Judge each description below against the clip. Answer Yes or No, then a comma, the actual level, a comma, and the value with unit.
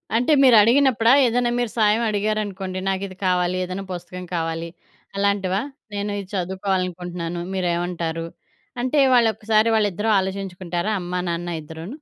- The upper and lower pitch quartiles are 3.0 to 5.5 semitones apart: Yes, average, 3.3 semitones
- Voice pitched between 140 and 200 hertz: Yes, high, 190 Hz